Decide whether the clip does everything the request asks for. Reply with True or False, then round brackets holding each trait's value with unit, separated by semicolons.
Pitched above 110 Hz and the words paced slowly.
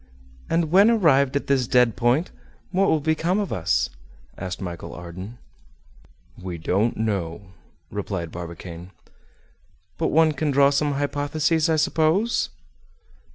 True (140 Hz; 125 wpm)